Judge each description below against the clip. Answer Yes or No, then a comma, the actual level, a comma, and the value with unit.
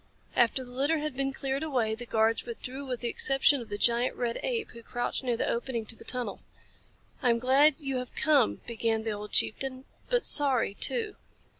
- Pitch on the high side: Yes, very high, 250 Hz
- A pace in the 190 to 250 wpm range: Yes, average, 200 wpm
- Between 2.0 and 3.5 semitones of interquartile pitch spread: Yes, average, 2.8 semitones